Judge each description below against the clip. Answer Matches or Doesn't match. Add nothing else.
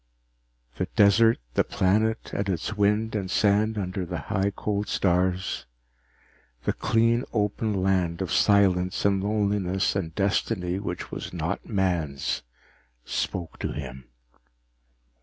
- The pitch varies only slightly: Matches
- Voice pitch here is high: Doesn't match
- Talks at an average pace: Doesn't match